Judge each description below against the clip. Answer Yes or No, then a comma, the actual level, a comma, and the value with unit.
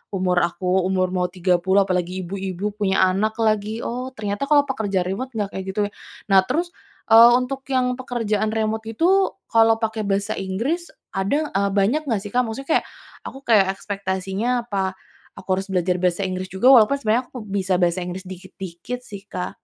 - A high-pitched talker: Yes, high, 200 Hz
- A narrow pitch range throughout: No, average, 3.3 semitones